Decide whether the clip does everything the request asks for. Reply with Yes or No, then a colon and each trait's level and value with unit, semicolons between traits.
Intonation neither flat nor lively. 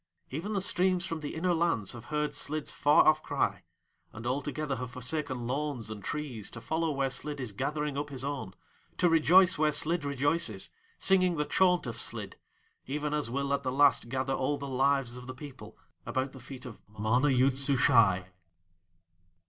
Yes: average, 3.2 semitones